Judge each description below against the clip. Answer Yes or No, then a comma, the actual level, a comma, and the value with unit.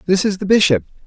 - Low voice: No, medium, 180 Hz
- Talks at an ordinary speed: No, fast, 225 wpm